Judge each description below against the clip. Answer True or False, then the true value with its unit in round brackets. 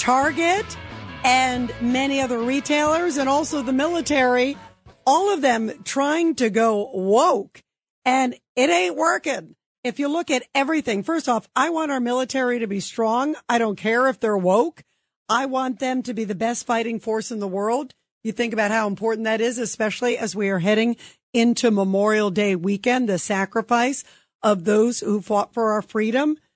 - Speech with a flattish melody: False (3.4 semitones)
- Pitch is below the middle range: False (240 Hz)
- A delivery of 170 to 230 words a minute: True (175 wpm)